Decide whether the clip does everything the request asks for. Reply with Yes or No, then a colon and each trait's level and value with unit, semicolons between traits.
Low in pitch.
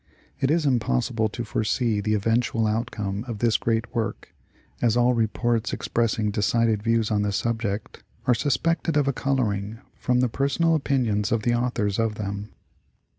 Yes: low, 115 Hz